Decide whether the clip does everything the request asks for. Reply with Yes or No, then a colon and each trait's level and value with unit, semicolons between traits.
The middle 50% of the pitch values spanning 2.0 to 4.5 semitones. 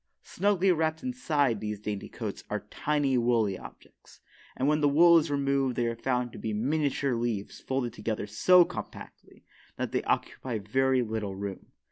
No: average, 5.3 semitones